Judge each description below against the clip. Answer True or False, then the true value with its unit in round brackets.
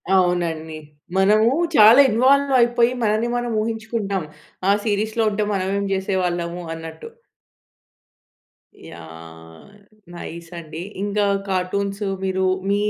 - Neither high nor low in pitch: False (195 Hz)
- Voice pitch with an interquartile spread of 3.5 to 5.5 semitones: True (4.2 semitones)